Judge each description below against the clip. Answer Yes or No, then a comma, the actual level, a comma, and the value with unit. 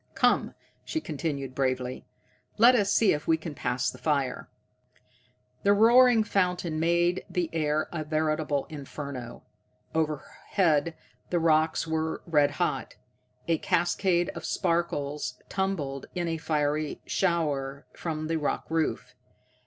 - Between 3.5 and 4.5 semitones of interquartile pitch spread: No, average, 2.9 semitones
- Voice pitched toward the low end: No, medium, 160 Hz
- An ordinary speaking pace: No, slow, 125 wpm